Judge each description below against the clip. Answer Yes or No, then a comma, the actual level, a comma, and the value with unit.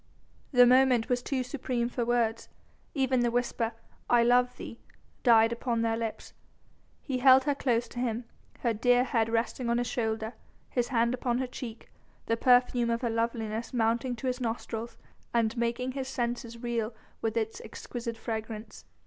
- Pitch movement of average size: No, narrow, 1.5 semitones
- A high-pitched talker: Yes, high, 235 Hz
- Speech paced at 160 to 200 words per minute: Yes, average, 165 wpm